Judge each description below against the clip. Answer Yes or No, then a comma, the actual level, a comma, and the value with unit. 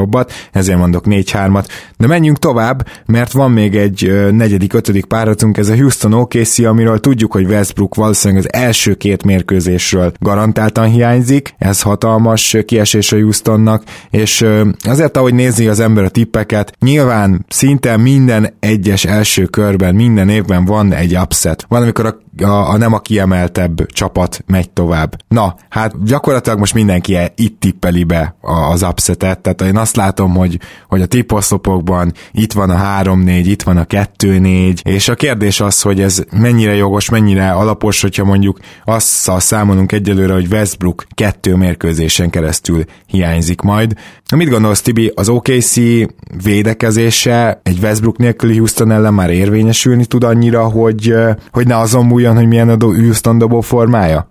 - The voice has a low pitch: Yes, low, 105 Hz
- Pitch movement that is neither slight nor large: Yes, average, 3.1 semitones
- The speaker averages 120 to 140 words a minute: No, fast, 155 wpm